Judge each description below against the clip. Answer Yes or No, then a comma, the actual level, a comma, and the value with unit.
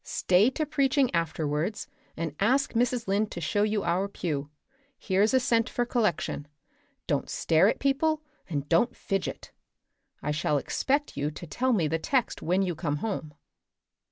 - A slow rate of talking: No, average, 160 wpm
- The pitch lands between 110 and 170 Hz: No, high, 195 Hz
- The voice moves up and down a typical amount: No, wide, 7.1 semitones